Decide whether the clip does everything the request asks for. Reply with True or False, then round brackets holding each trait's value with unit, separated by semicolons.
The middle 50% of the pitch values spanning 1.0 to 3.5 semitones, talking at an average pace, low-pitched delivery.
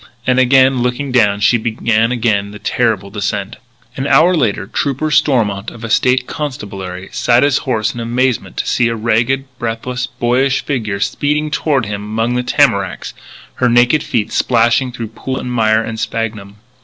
True (3.0 semitones; 170 wpm; 120 Hz)